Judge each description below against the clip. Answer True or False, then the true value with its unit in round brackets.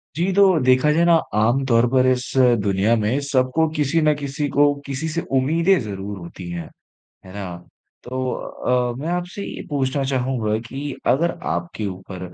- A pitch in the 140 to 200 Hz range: False (130 Hz)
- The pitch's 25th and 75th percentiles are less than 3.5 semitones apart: False (5.6 semitones)